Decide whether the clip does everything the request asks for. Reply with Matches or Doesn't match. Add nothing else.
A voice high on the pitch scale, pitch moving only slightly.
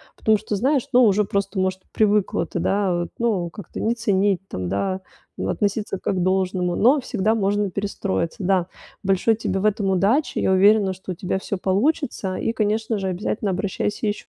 Matches